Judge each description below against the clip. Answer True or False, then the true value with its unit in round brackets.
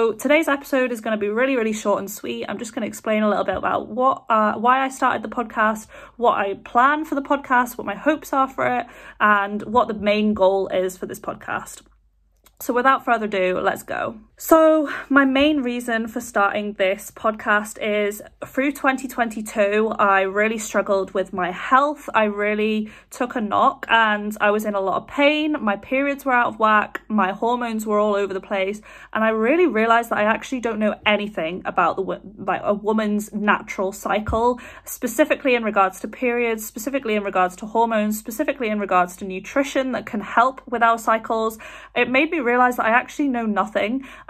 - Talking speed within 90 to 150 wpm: False (200 wpm)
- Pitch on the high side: True (225 Hz)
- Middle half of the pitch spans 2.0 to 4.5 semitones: True (3.9 semitones)